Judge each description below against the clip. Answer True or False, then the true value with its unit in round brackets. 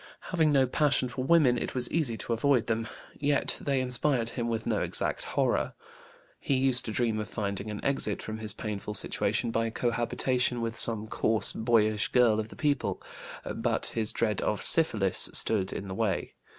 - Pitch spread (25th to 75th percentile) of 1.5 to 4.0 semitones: True (3.0 semitones)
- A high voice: False (115 Hz)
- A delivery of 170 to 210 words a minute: True (180 wpm)